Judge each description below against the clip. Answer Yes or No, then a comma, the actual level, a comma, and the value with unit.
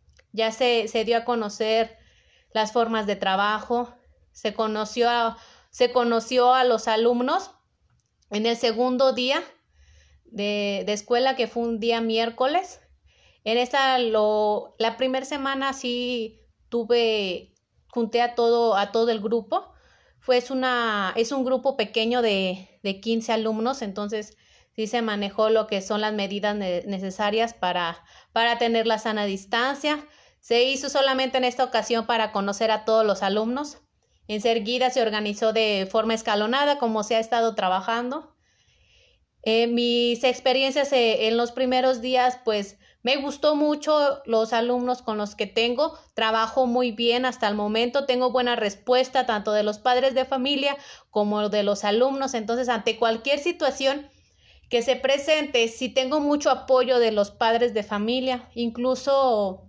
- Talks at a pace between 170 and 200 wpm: No, average, 150 wpm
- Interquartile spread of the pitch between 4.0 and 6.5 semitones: No, average, 2.9 semitones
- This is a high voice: Yes, high, 235 Hz